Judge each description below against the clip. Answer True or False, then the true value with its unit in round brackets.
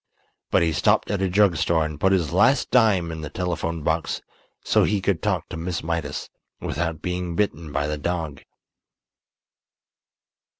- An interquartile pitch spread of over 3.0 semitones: False (2.7 semitones)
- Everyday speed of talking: True (165 wpm)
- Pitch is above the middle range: False (85 Hz)